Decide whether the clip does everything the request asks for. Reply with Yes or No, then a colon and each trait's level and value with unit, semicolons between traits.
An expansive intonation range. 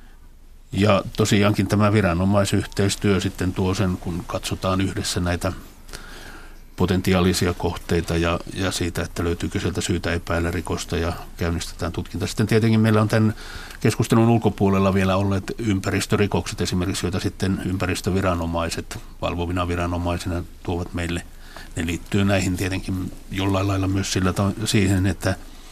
No: narrow, 2.5 semitones